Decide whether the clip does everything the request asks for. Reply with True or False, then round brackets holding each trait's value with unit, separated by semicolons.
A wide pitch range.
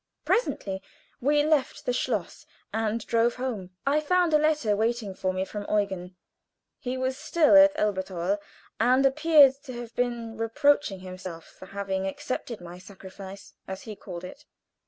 True (6.0 semitones)